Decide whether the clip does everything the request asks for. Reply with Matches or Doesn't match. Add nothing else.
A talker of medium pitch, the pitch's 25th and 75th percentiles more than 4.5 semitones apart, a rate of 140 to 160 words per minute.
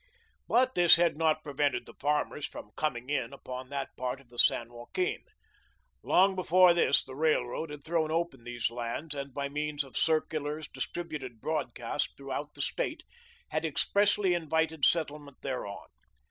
Doesn't match